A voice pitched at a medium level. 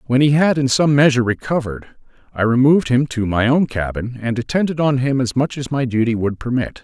No: low, 130 Hz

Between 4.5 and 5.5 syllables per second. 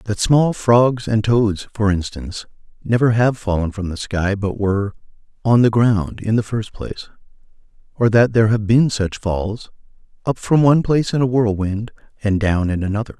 Yes: 5.0 syllables/s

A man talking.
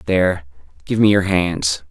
Yes: male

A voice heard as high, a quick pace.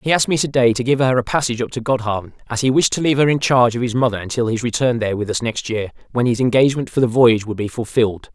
No: low, 120 Hz; fast, 295 wpm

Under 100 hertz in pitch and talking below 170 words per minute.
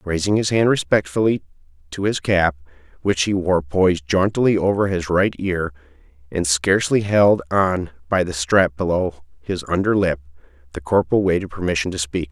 Yes: very low, 90 Hz; average, 160 wpm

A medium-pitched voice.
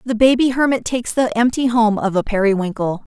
No: high, 230 Hz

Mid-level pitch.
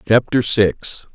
No: low, 110 Hz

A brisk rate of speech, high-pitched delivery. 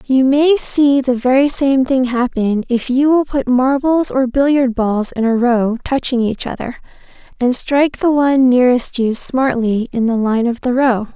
No: average, 190 wpm; very high, 255 Hz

